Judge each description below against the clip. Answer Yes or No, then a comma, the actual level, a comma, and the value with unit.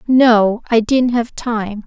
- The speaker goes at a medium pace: Yes, average, 160 wpm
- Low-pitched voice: No, high, 230 Hz